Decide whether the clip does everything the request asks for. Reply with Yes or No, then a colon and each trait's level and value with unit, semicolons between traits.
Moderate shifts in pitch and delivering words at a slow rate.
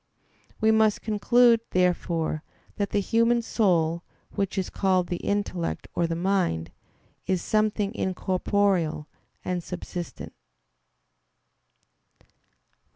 Yes: average, 3.4 semitones; slow, 95 wpm